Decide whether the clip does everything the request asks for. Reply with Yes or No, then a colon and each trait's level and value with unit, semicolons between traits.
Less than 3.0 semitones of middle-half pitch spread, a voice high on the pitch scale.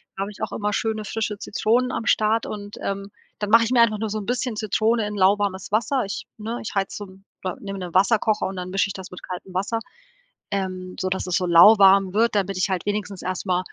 Yes: narrow, 2.4 semitones; high, 205 Hz